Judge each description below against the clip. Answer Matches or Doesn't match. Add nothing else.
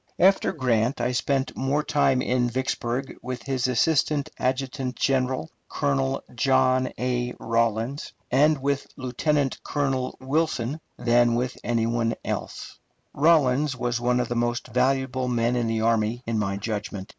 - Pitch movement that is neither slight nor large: Doesn't match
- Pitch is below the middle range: Matches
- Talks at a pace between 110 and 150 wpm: Matches